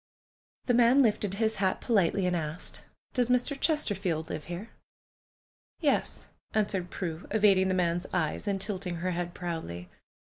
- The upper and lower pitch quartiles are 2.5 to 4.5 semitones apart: Yes, average, 3.9 semitones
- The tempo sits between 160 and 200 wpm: No, average, 150 wpm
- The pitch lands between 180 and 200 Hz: Yes, high, 190 Hz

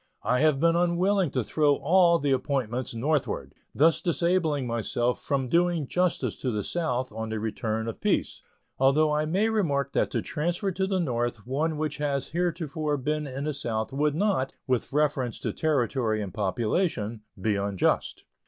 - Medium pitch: Yes, medium, 145 Hz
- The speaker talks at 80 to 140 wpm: No, average, 170 wpm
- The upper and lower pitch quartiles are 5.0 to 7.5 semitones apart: Yes, wide, 5.4 semitones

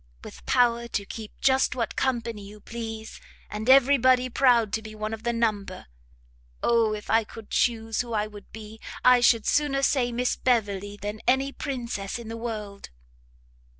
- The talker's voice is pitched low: No, high, 230 Hz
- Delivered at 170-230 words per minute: Yes, average, 175 wpm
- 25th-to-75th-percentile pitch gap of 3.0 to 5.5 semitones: No, narrow, 2.6 semitones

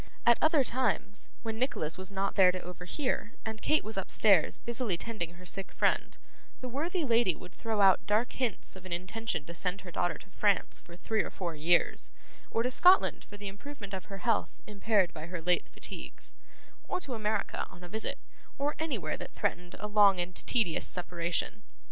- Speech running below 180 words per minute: No, average, 190 wpm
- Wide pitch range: No, average, 4.4 semitones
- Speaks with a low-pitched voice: No, high, 200 Hz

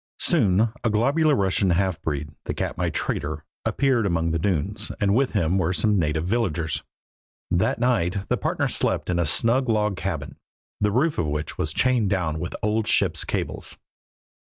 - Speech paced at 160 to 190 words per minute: Yes, average, 170 wpm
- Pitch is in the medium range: No, very low, 95 Hz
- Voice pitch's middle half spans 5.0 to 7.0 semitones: Yes, wide, 5.5 semitones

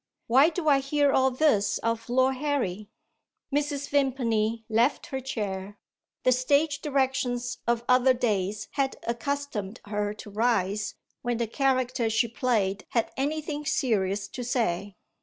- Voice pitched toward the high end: Yes, high, 245 Hz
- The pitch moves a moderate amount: Yes, average, 4.3 semitones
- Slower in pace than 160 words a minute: Yes, average, 140 wpm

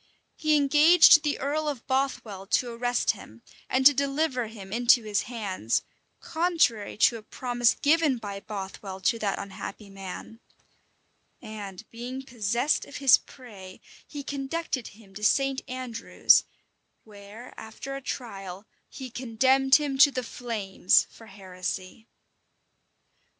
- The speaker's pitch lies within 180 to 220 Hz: No, high, 240 Hz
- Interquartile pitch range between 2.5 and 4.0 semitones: No, average, 5.1 semitones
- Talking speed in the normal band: No, slow, 130 wpm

